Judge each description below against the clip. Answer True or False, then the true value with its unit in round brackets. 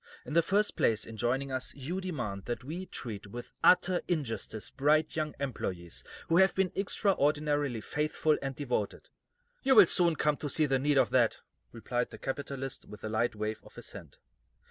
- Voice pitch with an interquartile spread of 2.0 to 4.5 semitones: False (5.0 semitones)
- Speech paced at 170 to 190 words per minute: True (185 wpm)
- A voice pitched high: False (140 Hz)